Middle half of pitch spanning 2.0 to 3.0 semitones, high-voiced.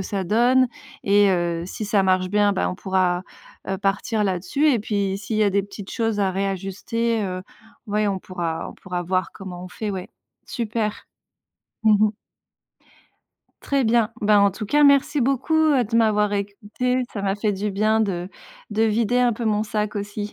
Yes: narrow, 2.6 semitones; high, 205 Hz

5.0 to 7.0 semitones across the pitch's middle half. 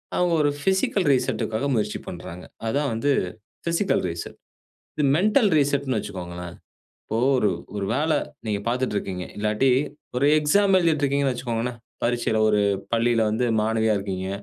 Yes: wide, 5.4 semitones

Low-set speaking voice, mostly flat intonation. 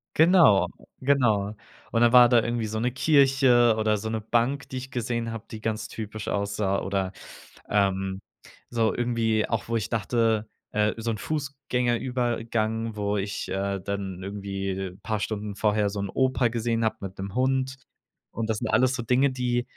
No: low, 110 Hz; average, 3.0 semitones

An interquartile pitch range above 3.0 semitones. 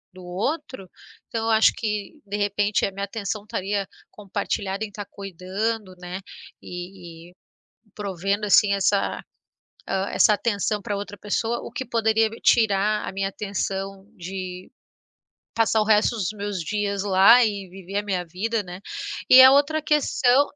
No: narrow, 2.4 semitones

